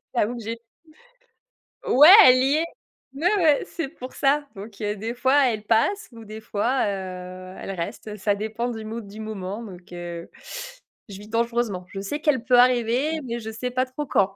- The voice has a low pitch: No, high, 225 Hz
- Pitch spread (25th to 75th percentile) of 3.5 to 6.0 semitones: Yes, average, 4.0 semitones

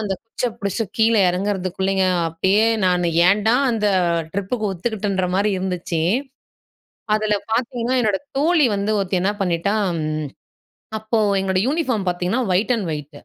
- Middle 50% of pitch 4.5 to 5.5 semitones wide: No, average, 3.2 semitones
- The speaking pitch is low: No, high, 200 Hz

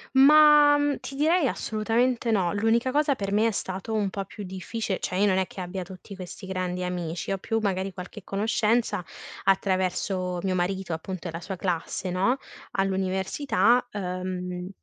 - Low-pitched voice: No, high, 195 Hz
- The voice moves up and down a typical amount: Yes, average, 3.6 semitones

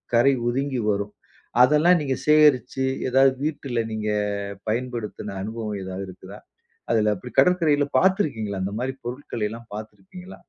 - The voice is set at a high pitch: No, low, 120 Hz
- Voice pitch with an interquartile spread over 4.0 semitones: Yes, average, 5.2 semitones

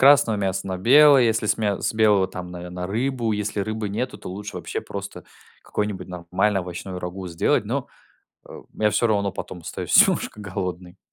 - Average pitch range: Yes, average, 3.0 semitones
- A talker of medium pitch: No, low, 100 Hz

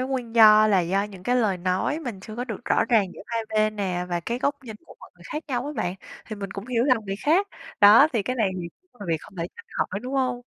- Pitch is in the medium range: No, high, 215 Hz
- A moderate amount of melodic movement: Yes, average, 4.2 semitones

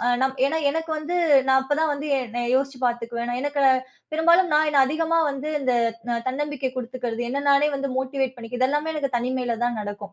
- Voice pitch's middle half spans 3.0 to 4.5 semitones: Yes, average, 3.3 semitones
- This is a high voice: Yes, very high, 270 Hz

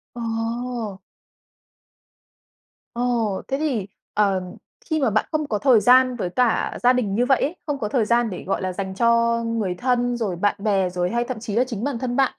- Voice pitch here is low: No, high, 235 Hz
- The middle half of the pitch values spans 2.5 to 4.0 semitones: Yes, average, 3.4 semitones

